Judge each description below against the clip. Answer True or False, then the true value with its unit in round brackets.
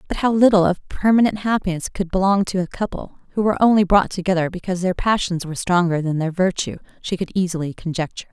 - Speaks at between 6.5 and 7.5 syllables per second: True (6.6 syllables/s)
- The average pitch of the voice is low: False (185 Hz)